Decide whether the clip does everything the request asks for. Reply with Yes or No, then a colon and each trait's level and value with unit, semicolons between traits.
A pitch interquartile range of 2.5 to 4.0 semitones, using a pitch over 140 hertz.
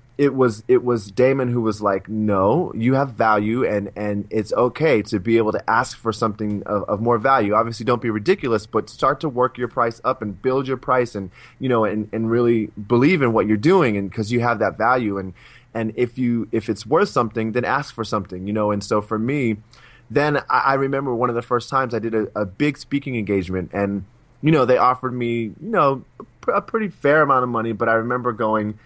No: average, 3.0 semitones; low, 115 Hz